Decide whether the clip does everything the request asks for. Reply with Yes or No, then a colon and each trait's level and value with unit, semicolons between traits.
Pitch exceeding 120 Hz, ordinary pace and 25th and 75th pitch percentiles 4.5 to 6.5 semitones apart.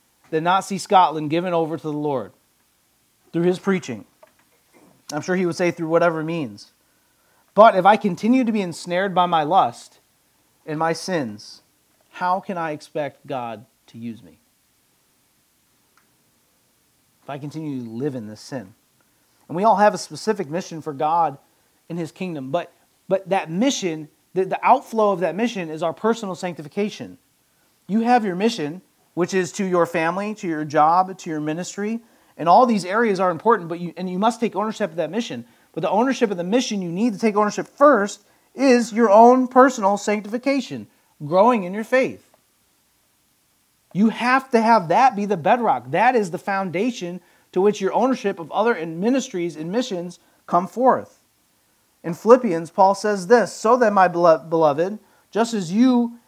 Yes: high, 190 Hz; average, 175 wpm; average, 5.0 semitones